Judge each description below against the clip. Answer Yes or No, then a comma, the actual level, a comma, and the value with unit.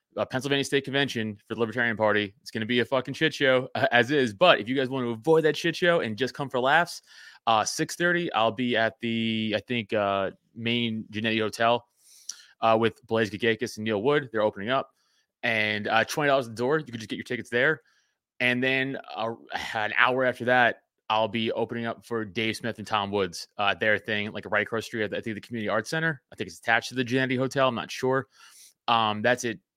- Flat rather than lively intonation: No, average, 3.1 semitones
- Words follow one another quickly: Yes, fast, 230 wpm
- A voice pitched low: Yes, low, 115 Hz